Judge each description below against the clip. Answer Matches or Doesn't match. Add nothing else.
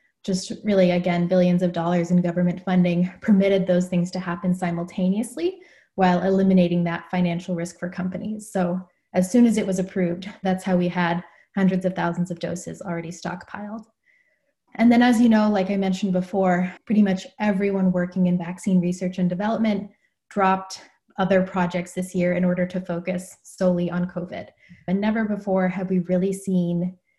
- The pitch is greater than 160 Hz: Matches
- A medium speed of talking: Matches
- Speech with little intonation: Matches